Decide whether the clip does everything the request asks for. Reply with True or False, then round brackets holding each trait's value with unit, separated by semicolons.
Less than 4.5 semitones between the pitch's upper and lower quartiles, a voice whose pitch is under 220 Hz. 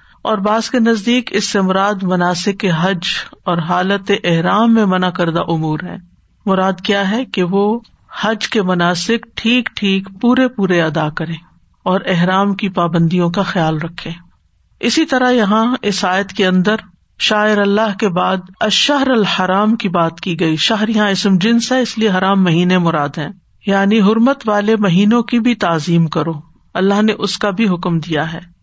True (3.5 semitones; 195 Hz)